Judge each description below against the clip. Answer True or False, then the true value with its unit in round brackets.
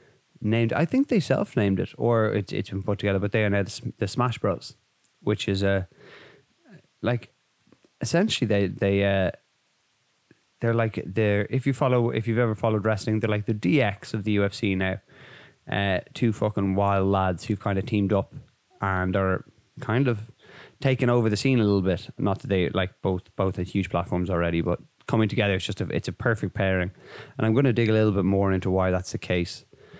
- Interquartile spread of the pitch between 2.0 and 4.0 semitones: True (3.4 semitones)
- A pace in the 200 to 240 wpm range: True (205 wpm)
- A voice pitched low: True (105 Hz)